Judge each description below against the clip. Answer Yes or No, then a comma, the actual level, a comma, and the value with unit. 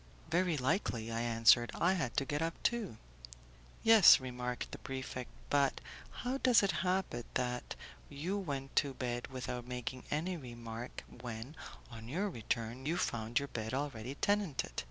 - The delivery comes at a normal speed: Yes, average, 155 wpm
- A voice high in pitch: No, low, 130 Hz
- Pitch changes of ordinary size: No, wide, 6.0 semitones